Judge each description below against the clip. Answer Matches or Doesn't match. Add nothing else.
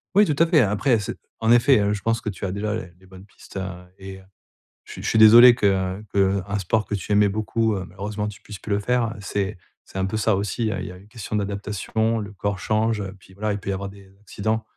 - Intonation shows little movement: Matches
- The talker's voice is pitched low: Matches